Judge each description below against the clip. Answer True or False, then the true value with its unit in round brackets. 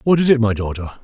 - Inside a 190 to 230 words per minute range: False (290 wpm)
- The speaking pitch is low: True (120 Hz)